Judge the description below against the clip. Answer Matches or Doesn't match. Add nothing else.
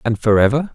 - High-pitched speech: Doesn't match